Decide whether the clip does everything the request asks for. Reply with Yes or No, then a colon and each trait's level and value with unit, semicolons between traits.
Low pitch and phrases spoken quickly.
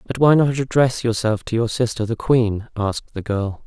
Yes: low, 115 Hz; fast, 215 wpm